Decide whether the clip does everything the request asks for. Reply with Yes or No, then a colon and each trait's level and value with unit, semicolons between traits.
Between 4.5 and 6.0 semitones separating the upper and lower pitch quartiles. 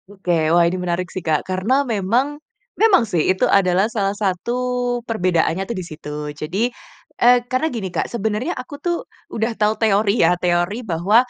Yes: average, 5.0 semitones